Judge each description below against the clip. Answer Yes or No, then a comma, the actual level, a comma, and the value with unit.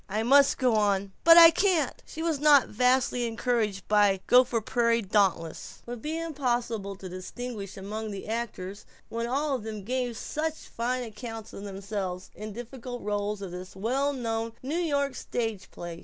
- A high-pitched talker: Yes, high, 230 Hz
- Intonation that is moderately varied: Yes, average, 4.0 semitones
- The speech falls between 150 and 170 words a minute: Yes, average, 165 wpm